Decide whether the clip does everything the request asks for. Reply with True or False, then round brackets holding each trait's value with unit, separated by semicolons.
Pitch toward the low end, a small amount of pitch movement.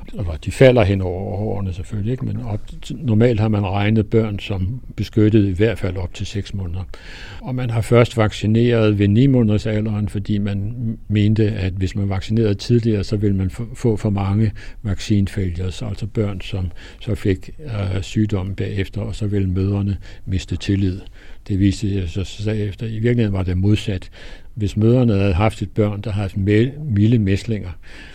True (105 Hz; 2.2 semitones)